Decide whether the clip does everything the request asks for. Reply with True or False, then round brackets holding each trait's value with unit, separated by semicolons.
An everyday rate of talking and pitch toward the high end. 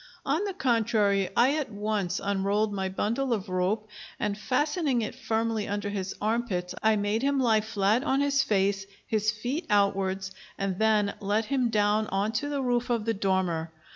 True (180 wpm; 215 Hz)